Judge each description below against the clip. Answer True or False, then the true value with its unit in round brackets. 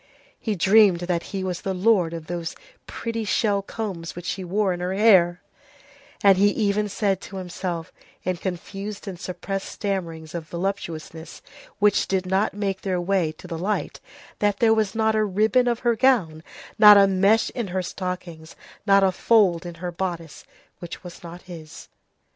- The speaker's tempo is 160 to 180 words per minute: True (175 wpm)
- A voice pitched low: False (190 Hz)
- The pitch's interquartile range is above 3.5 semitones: False (2.9 semitones)